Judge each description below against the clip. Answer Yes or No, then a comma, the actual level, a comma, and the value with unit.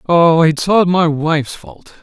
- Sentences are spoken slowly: No, fast, 205 wpm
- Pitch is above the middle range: No, medium, 165 Hz